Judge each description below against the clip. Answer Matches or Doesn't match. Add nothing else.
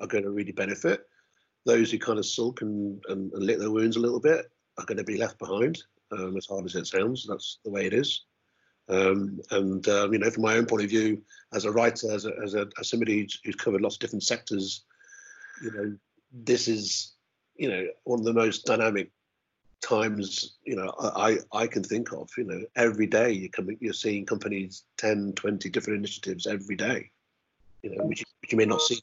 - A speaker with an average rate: Doesn't match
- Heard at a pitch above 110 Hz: Doesn't match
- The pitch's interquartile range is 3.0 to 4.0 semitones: Doesn't match